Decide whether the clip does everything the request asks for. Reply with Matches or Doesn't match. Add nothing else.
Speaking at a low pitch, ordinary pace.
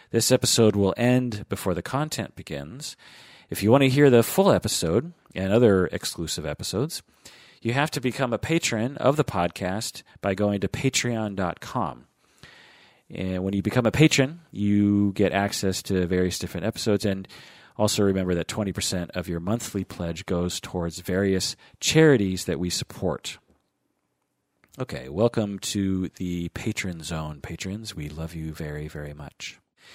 Matches